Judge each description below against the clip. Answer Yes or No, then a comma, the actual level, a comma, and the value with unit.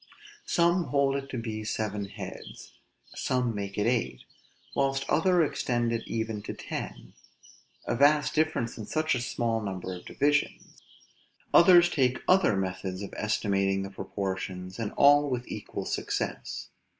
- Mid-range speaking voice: No, low, 120 Hz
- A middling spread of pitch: No, wide, 5.9 semitones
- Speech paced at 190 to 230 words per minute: No, average, 145 wpm